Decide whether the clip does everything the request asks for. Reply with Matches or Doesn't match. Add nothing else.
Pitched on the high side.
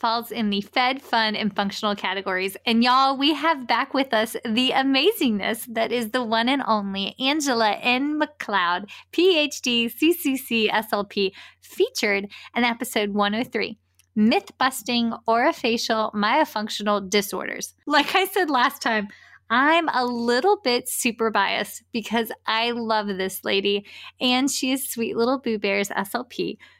Matches